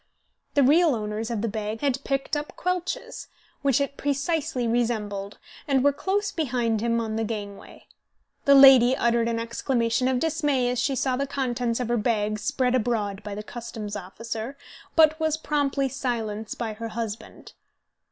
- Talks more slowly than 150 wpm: No, average, 165 wpm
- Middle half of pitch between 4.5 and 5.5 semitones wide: No, average, 3.9 semitones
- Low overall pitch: No, high, 245 Hz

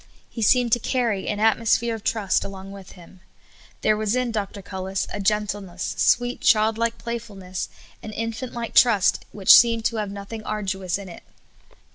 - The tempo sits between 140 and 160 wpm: No, average, 175 wpm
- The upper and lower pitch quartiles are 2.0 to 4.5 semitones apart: Yes, average, 2.8 semitones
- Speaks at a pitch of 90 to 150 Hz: No, high, 215 Hz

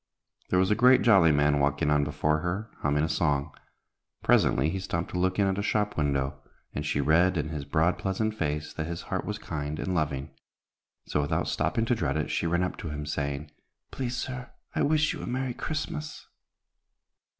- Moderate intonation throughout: No, wide, 6.0 semitones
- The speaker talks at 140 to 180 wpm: No, average, 200 wpm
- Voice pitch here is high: No, very low, 80 Hz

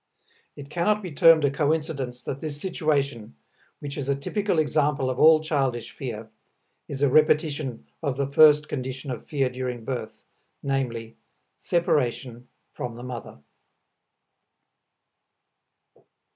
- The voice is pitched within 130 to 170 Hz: Yes, medium, 140 Hz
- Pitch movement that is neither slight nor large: Yes, average, 3.4 semitones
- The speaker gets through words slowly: Yes, slow, 125 wpm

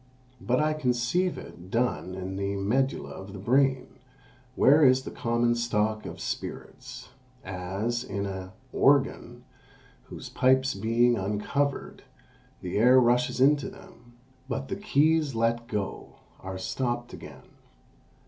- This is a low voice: Yes, low, 120 Hz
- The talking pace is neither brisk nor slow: No, slow, 130 wpm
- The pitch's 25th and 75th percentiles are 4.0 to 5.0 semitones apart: Yes, average, 4.7 semitones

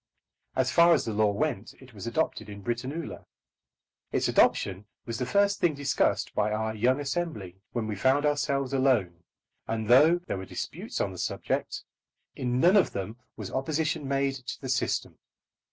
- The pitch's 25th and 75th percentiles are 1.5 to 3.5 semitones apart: No, average, 5.0 semitones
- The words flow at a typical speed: Yes, average, 170 wpm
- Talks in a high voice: No, low, 130 Hz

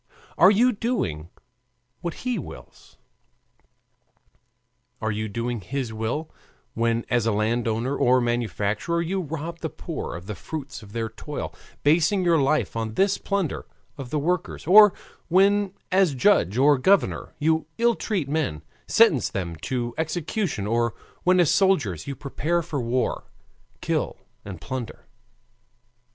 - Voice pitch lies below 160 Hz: Yes, medium, 140 Hz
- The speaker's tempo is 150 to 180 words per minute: No, average, 140 wpm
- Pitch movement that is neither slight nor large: No, wide, 7.4 semitones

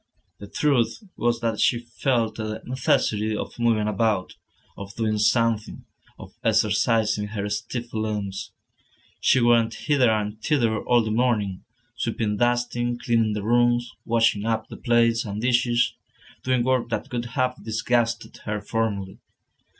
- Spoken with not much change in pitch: Yes, narrow, 2.0 semitones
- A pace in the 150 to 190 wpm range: No, average, 140 wpm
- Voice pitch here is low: Yes, low, 115 Hz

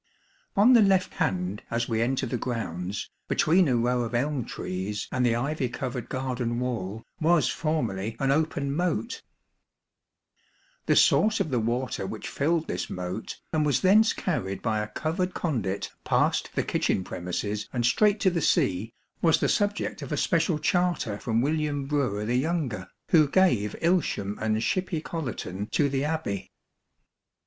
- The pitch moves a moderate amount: No, wide, 6.7 semitones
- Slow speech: No, average, 160 wpm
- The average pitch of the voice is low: Yes, low, 130 Hz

